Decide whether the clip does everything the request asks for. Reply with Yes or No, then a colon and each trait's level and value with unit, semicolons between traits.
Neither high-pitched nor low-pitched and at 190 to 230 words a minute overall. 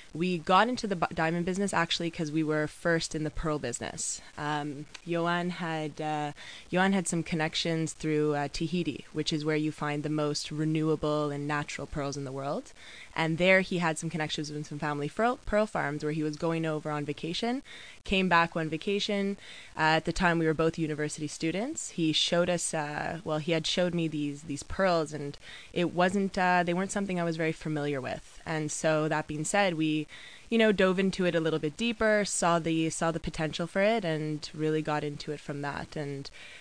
Yes: medium, 160 Hz; fast, 205 wpm